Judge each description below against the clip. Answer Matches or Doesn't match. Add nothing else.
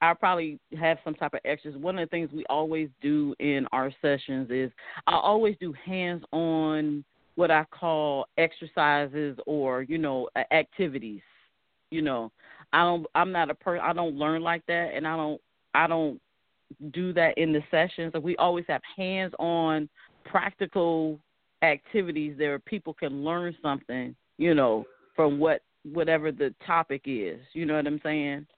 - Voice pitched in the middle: Matches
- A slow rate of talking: Doesn't match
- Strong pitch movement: Doesn't match